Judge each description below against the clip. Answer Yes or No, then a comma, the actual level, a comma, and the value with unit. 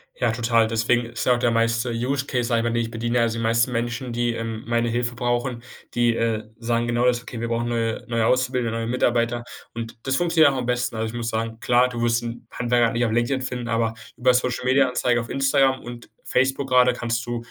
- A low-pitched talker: Yes, low, 120 Hz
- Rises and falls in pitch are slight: Yes, narrow, 1.3 semitones